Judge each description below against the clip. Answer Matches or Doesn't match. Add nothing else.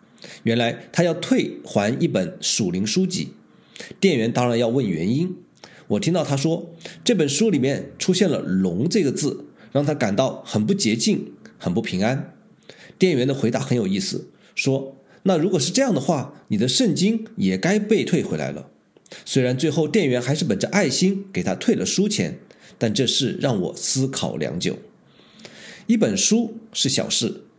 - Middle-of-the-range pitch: Matches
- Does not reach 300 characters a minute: Matches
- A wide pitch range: Matches